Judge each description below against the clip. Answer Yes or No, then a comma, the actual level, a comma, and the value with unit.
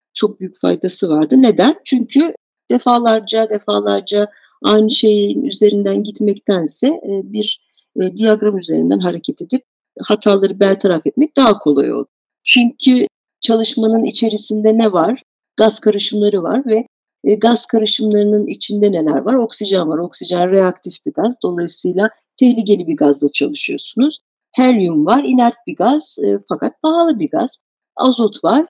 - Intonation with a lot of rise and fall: No, average, 4.3 semitones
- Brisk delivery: No, average, 125 wpm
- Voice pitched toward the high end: Yes, high, 215 Hz